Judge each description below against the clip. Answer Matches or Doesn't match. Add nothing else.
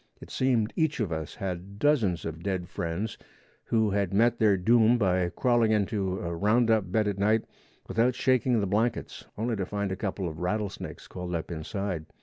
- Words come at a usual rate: Matches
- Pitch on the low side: Matches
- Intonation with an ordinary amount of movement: Matches